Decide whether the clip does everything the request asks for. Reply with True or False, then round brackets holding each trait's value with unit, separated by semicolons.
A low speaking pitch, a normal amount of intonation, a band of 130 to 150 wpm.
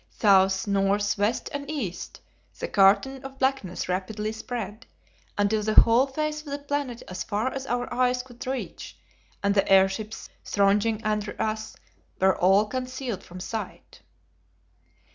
False (220 Hz; 4.3 semitones; 145 wpm)